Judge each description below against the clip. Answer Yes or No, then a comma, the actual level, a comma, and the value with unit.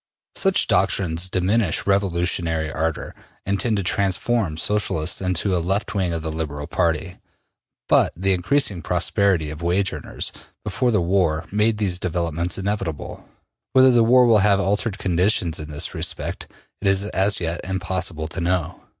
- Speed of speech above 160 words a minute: No, average, 155 wpm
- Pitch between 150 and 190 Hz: No, very low, 90 Hz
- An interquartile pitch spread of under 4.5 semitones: Yes, average, 3.2 semitones